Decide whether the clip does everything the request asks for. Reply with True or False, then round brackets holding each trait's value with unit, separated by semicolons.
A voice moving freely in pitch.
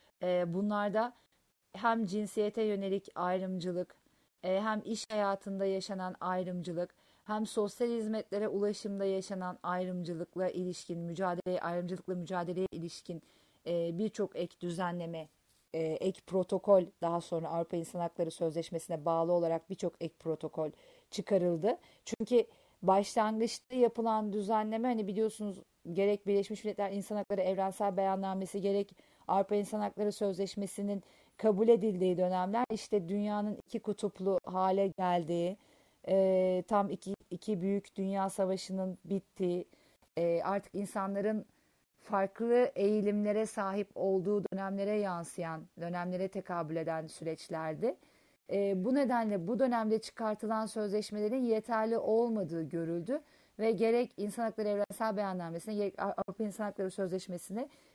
False (2.9 semitones)